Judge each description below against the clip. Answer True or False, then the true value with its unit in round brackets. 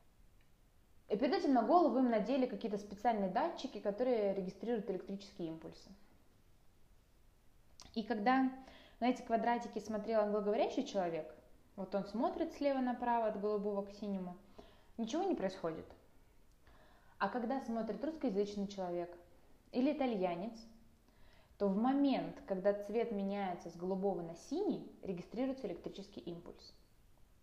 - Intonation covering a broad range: False (4.4 semitones)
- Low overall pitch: False (215 Hz)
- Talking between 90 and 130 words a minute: True (120 wpm)